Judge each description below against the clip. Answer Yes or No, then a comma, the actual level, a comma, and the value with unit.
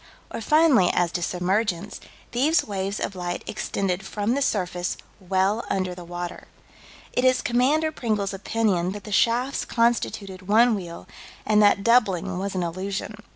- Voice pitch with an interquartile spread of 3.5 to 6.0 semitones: Yes, average, 4.1 semitones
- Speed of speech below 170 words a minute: Yes, average, 155 wpm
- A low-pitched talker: No, high, 200 Hz